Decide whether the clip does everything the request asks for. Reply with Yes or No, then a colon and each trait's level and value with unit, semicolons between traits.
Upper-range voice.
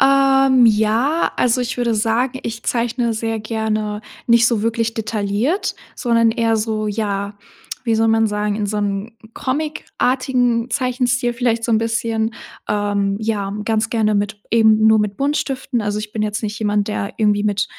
Yes: high, 225 Hz